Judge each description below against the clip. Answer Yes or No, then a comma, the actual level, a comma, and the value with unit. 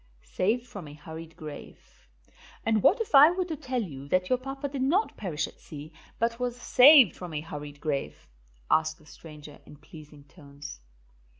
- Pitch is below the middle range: No, medium, 170 Hz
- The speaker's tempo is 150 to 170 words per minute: No, average, 180 wpm